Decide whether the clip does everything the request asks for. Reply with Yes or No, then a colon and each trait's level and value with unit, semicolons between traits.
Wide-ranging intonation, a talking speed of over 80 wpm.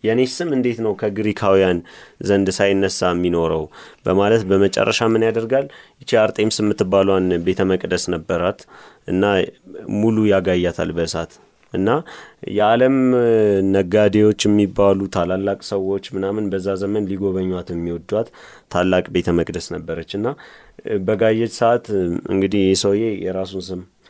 No: average, 2.7 semitones; fast, 110 wpm